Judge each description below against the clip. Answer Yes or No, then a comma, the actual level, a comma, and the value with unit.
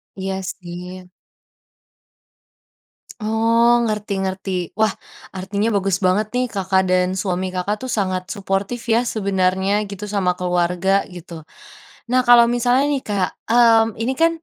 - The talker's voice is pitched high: Yes, high, 195 Hz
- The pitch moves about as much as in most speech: Yes, average, 3.3 semitones